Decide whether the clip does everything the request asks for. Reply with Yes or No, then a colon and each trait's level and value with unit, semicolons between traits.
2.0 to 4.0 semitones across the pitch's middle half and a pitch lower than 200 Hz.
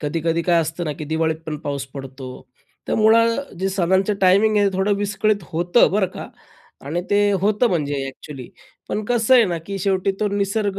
No: average, 4.5 semitones; high, 190 Hz